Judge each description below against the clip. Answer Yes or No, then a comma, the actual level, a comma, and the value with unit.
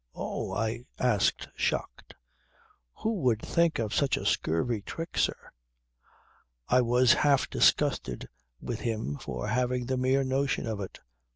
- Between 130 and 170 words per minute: Yes, slow, 135 wpm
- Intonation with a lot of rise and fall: No, average, 3.1 semitones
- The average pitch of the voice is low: Yes, low, 125 Hz